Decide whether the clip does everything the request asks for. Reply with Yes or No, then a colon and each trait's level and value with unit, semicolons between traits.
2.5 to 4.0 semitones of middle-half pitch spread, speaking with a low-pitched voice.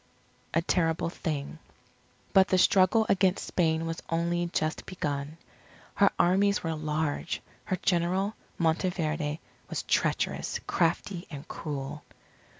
No: average, 2.9 semitones; medium, 165 Hz